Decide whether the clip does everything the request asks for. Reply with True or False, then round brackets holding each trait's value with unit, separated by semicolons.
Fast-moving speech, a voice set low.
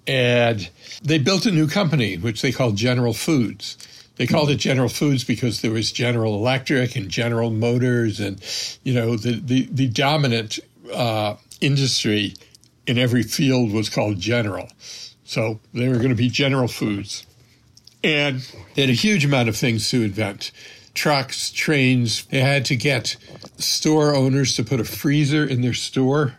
False (165 wpm; 125 Hz)